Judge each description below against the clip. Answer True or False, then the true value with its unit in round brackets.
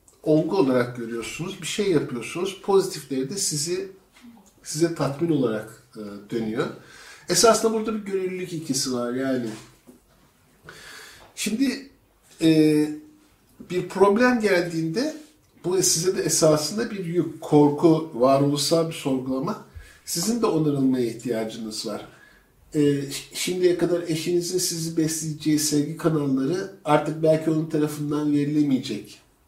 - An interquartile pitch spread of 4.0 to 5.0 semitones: True (4.4 semitones)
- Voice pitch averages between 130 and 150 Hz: False (160 Hz)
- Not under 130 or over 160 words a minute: False (110 wpm)